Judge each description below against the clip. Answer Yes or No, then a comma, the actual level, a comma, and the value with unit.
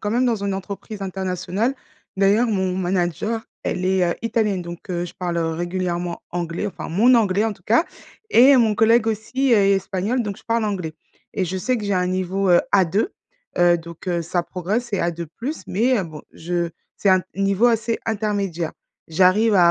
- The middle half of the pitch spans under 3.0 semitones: No, average, 3.8 semitones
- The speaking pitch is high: Yes, high, 195 Hz